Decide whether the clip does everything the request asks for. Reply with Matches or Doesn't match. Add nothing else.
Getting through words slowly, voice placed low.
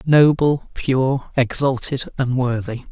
Matches